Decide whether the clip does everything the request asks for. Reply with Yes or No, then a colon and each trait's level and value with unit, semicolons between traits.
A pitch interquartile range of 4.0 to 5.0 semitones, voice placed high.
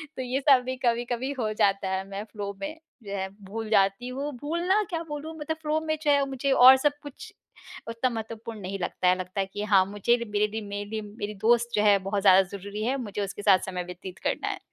Yes: average, 4.7 semitones; high, 220 Hz